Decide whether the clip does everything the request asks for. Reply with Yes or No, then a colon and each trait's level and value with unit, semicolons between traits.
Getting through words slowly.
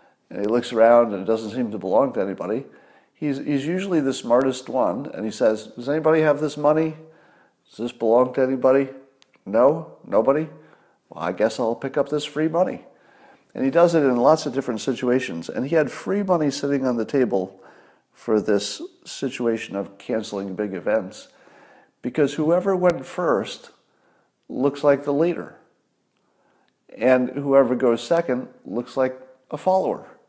No: average, 165 wpm